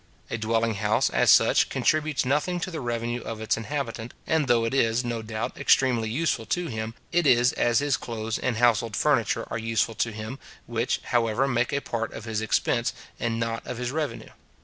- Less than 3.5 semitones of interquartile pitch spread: Yes, average, 2.9 semitones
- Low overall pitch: Yes, low, 120 Hz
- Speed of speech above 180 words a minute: Yes, average, 195 wpm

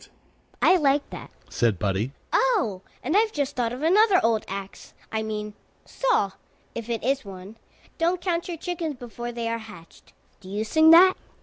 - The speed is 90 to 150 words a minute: No, average, 175 wpm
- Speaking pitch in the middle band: No, high, 240 Hz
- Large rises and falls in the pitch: Yes, wide, 8.1 semitones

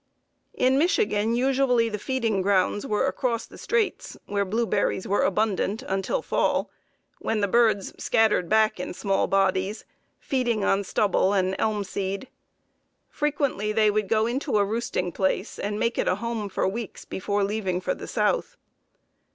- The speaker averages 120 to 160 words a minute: Yes, average, 155 wpm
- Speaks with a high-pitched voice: Yes, high, 215 Hz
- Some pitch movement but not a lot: Yes, average, 3.2 semitones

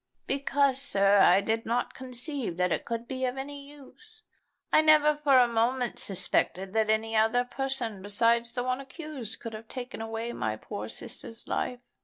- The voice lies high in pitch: Yes, high, 240 Hz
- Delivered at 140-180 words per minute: Yes, average, 175 wpm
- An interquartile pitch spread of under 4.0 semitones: Yes, average, 3.5 semitones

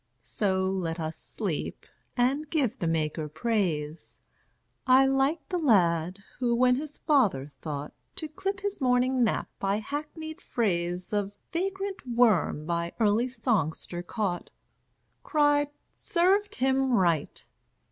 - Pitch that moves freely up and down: Yes, wide, 8.7 semitones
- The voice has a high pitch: Yes, high, 235 Hz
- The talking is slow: Yes, slow, 125 wpm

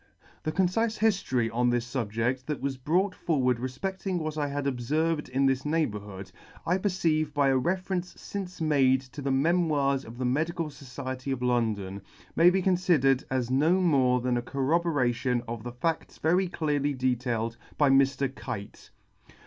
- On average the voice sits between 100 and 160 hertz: Yes, medium, 140 Hz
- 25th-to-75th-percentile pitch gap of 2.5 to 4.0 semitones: No, average, 4.7 semitones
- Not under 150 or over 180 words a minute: Yes, average, 165 wpm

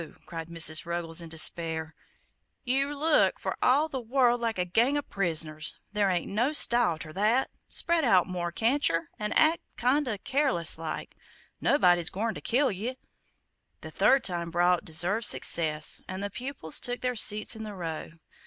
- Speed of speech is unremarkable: Yes, average, 170 wpm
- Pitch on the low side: No, high, 205 Hz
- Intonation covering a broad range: Yes, wide, 7.0 semitones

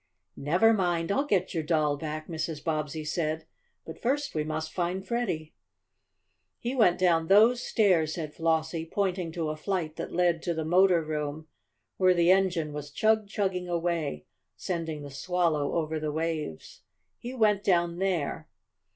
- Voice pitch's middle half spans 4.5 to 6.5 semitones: No, average, 3.3 semitones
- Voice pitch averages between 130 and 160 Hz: No, medium, 170 Hz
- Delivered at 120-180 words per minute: Yes, average, 160 wpm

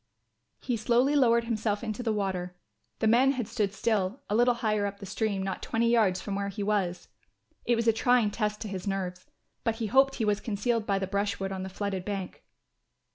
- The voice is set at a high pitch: Yes, high, 210 Hz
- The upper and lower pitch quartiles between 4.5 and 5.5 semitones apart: No, average, 2.9 semitones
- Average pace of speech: No, fast, 210 wpm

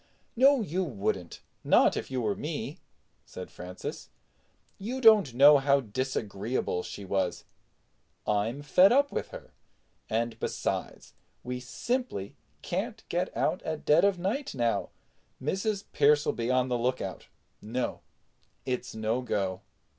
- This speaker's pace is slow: Yes, slow, 130 wpm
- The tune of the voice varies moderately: No, wide, 8.9 semitones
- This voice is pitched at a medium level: No, low, 130 Hz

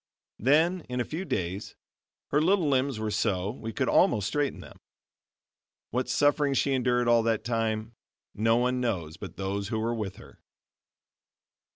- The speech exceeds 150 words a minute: Yes, average, 160 wpm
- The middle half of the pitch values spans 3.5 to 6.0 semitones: Yes, average, 4.2 semitones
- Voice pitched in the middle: No, low, 120 Hz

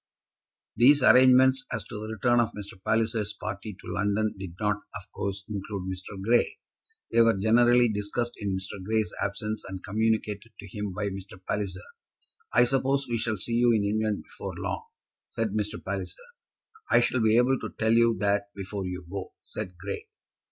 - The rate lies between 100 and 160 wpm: No, average, 175 wpm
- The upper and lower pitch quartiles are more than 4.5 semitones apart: No, average, 2.8 semitones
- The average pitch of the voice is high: No, low, 105 Hz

